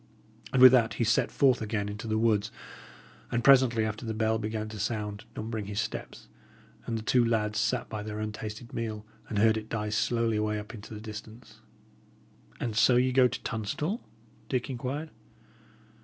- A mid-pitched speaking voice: No, low, 110 Hz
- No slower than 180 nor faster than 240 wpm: Yes, average, 185 wpm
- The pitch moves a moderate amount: No, narrow, 2.0 semitones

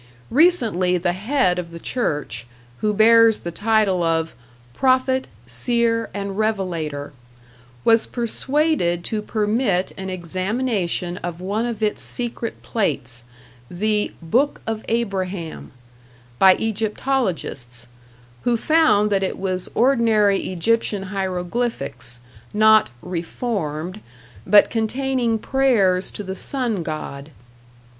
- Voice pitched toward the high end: Yes, high, 205 Hz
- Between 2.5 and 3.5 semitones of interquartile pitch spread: No, average, 4.6 semitones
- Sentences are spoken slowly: Yes, slow, 105 wpm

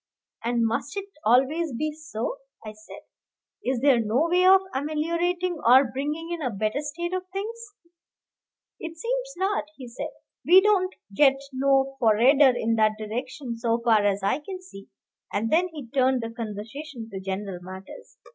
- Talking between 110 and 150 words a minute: No, average, 165 wpm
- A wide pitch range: Yes, wide, 6.8 semitones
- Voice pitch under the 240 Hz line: No, very high, 270 Hz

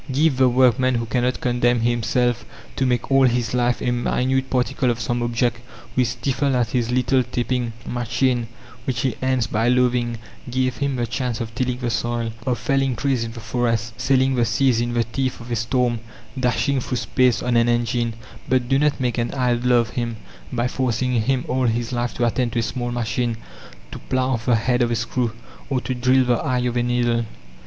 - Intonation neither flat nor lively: No, narrow, 1.4 semitones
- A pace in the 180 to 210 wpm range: Yes, fast, 205 wpm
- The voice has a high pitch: No, low, 120 Hz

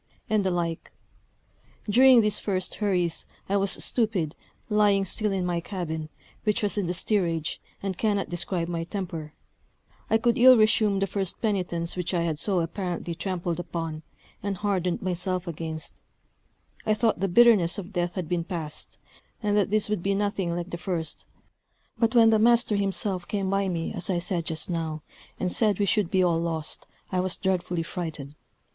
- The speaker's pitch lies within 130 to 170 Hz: No, medium, 185 Hz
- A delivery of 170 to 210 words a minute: Yes, average, 175 wpm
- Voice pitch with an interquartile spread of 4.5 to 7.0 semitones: No, average, 3.3 semitones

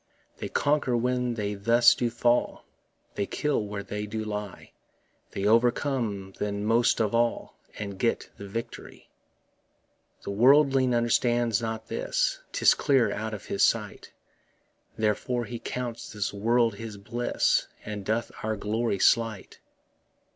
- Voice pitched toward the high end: No, low, 115 Hz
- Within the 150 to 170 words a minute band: No, slow, 135 wpm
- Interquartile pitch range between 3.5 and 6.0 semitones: No, narrow, 2.6 semitones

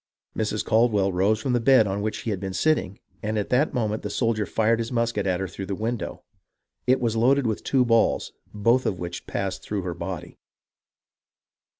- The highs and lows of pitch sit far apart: No, average, 3.2 semitones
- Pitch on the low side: Yes, low, 110 Hz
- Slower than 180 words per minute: No, average, 200 wpm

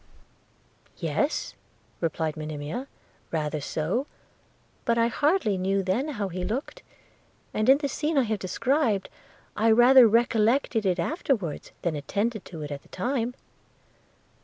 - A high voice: Yes, high, 215 Hz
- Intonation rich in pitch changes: Yes, wide, 6.3 semitones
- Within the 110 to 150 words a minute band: Yes, slow, 135 wpm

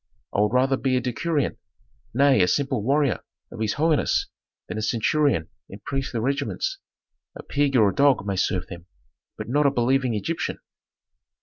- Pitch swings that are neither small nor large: Yes, average, 4.8 semitones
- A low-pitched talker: Yes, low, 130 Hz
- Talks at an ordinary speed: Yes, average, 170 wpm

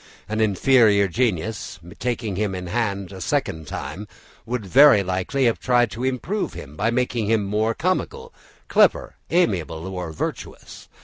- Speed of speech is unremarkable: Yes, average, 145 wpm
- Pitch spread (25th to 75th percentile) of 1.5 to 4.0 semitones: No, average, 4.8 semitones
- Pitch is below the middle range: Yes, low, 110 Hz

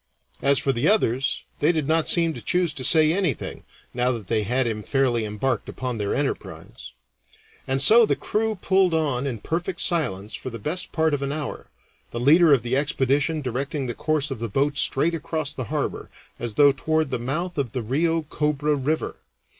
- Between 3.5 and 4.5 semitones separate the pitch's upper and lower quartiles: Yes, average, 4.1 semitones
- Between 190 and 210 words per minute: Yes, average, 195 wpm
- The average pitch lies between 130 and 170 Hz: Yes, medium, 140 Hz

